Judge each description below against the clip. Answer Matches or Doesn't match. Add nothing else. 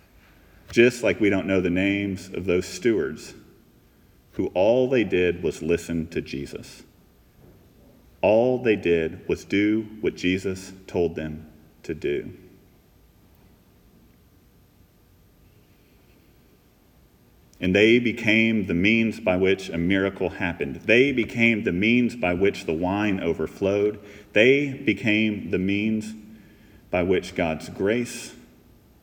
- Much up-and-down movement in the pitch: Doesn't match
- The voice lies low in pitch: Matches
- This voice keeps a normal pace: Doesn't match